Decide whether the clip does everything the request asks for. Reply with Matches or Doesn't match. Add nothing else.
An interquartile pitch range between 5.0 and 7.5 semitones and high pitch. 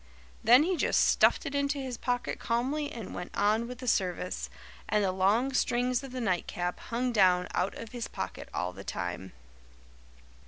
Matches